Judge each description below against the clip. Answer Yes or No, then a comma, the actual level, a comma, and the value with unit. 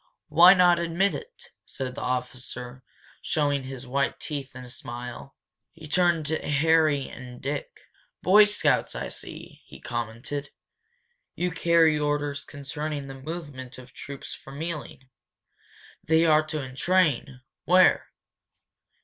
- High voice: No, medium, 145 Hz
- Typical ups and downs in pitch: Yes, average, 3.9 semitones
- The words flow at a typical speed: No, slow, 130 wpm